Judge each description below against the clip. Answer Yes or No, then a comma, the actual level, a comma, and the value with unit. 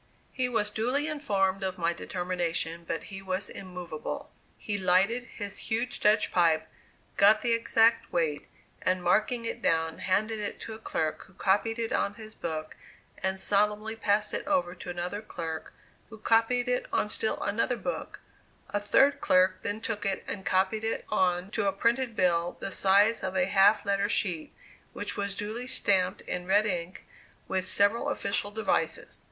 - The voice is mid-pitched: No, high, 200 Hz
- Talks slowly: No, average, 170 wpm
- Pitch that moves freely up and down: No, average, 3.3 semitones